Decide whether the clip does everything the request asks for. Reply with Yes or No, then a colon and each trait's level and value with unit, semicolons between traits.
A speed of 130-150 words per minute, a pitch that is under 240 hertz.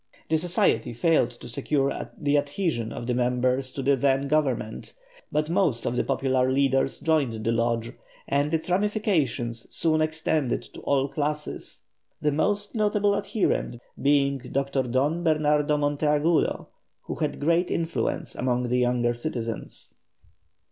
Yes: average, 140 wpm; medium, 140 Hz